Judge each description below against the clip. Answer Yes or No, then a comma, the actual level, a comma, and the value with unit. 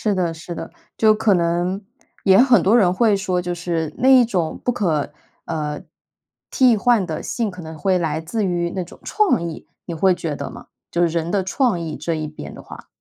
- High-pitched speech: No, medium, 180 Hz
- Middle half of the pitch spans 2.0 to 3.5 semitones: No, average, 4.1 semitones